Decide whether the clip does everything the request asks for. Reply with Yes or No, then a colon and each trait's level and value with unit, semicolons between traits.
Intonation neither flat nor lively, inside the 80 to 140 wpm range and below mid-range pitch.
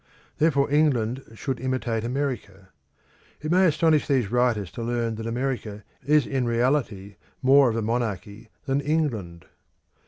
Yes: average, 4.1 semitones; slow, 135 wpm; low, 125 Hz